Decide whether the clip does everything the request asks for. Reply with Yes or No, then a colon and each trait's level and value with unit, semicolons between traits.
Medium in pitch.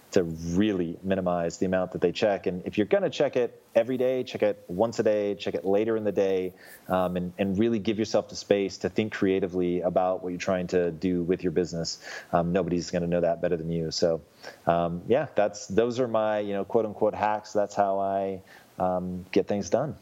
No: very low, 95 Hz